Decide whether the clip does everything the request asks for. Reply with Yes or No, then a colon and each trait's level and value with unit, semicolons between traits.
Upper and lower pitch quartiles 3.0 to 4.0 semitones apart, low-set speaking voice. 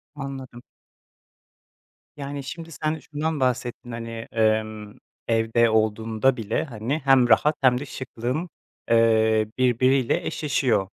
Yes: average, 3.6 semitones; low, 125 Hz